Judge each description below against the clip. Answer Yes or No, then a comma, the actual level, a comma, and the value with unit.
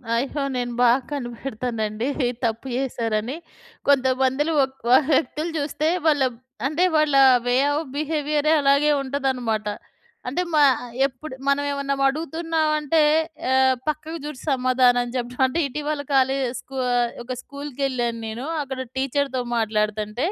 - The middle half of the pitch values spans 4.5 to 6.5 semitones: No, average, 3.1 semitones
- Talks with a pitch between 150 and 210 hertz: No, very high, 270 Hz